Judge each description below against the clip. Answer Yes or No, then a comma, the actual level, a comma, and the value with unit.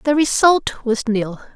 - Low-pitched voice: No, very high, 250 Hz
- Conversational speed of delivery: Yes, average, 155 wpm